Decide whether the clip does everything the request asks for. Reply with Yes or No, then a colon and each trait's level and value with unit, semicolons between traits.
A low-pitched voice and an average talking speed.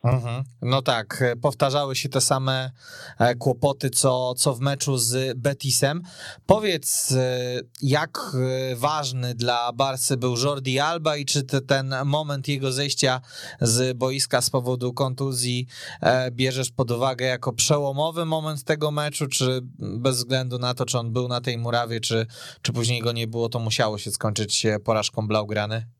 Yes: low, 130 Hz; average, 150 wpm